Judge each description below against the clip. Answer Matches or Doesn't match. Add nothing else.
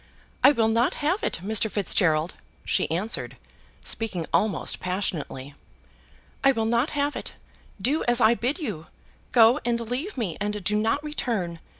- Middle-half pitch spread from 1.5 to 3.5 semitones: Doesn't match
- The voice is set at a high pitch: Matches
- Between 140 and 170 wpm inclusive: Matches